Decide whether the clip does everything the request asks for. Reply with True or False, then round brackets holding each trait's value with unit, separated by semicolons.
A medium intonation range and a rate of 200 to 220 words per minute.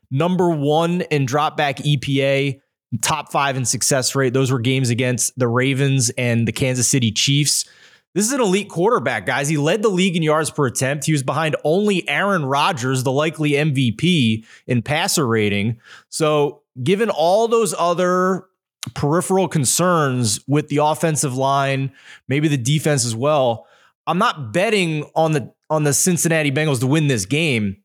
False (3.7 semitones; 165 wpm)